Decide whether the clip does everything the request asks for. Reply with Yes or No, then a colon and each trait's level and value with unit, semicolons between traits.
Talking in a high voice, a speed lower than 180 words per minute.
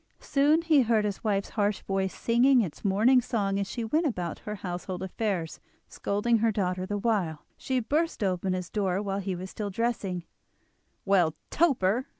Yes: high, 205 Hz; average, 170 wpm